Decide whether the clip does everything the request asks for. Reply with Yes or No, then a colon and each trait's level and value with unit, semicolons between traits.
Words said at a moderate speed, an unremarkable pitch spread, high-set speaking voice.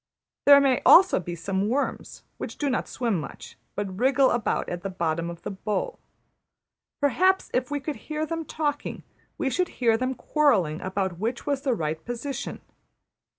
No: average, 170 wpm; wide, 7.2 semitones; high, 245 Hz